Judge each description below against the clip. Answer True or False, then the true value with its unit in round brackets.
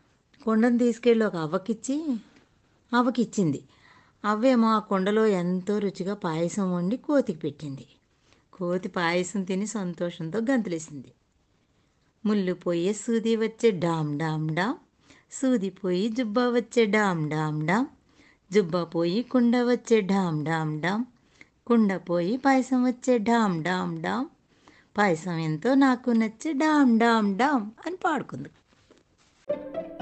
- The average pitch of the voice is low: False (210 Hz)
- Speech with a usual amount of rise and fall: False (5.7 semitones)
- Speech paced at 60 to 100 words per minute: False (110 wpm)